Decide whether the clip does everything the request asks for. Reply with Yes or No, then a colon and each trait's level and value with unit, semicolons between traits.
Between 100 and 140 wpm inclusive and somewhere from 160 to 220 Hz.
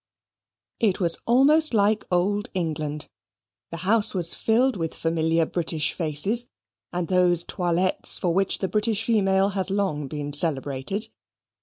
Yes: slow, 135 wpm; medium, 185 Hz